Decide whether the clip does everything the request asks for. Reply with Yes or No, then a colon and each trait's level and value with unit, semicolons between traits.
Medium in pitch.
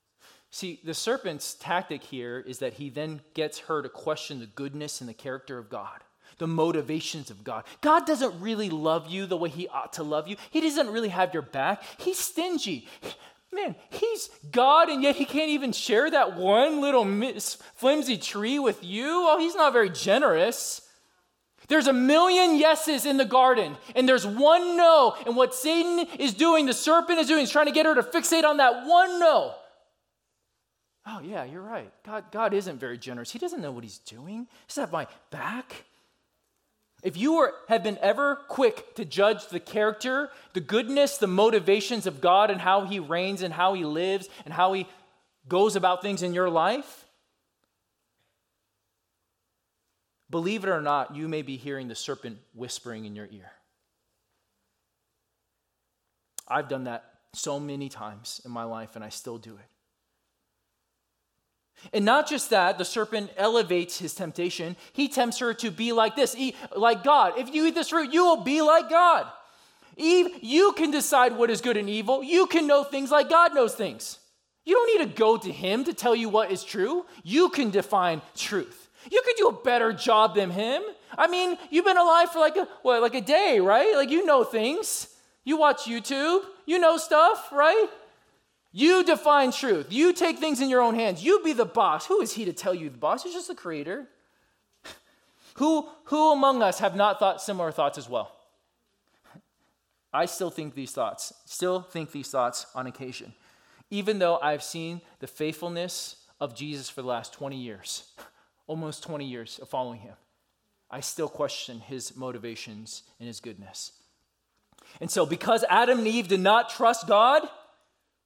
No: high, 215 Hz